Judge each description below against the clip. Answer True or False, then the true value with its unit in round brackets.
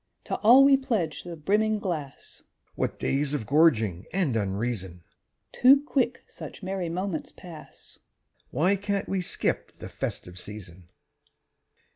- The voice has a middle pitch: True (165 Hz)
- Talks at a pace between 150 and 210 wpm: False (135 wpm)